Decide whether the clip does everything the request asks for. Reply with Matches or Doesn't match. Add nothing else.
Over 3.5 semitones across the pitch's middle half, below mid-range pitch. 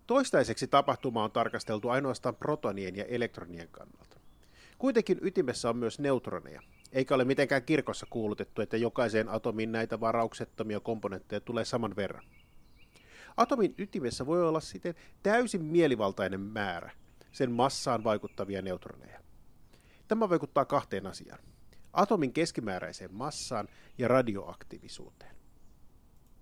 Matches